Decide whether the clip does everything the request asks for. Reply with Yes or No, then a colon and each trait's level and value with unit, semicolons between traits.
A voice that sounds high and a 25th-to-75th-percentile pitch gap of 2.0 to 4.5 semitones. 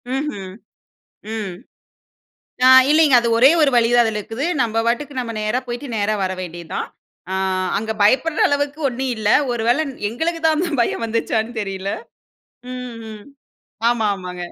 Yes: high, 230 Hz; average, 4.1 semitones